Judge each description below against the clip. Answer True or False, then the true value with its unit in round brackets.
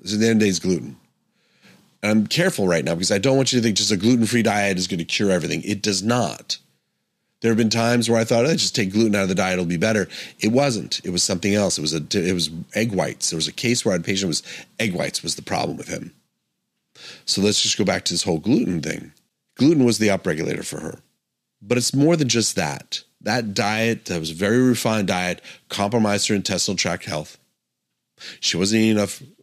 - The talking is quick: True (250 wpm)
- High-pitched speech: False (105 Hz)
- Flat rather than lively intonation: False (3.8 semitones)